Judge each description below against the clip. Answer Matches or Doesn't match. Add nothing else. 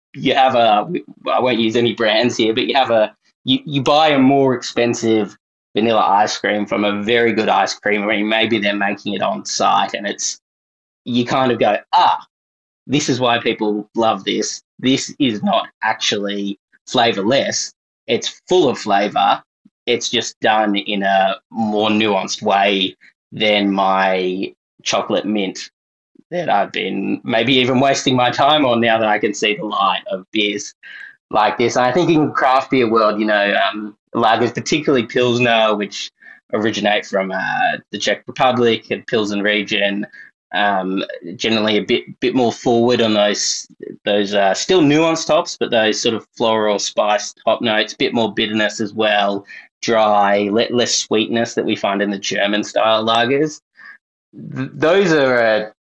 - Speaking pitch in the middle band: Doesn't match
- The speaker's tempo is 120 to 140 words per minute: Doesn't match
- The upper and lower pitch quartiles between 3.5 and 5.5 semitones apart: Doesn't match